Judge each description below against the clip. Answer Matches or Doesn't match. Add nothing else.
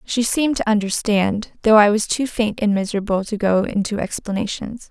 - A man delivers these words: Doesn't match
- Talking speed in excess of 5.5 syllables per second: Doesn't match